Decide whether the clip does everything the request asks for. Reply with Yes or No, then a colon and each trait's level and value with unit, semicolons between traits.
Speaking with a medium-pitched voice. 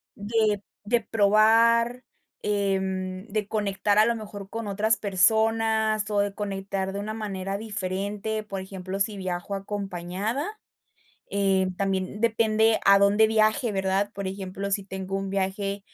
No: high, 200 Hz